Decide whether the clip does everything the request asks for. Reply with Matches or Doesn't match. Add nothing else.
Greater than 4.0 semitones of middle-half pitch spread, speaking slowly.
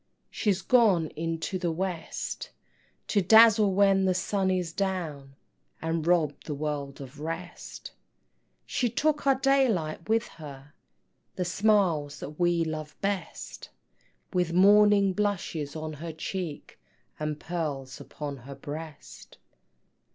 Matches